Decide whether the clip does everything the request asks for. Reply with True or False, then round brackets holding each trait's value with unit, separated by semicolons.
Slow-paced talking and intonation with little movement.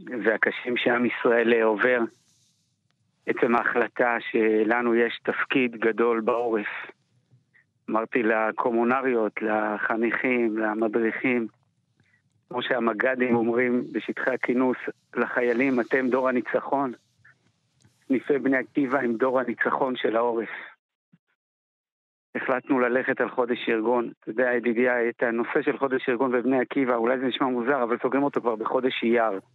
False (115 wpm; 2.0 semitones)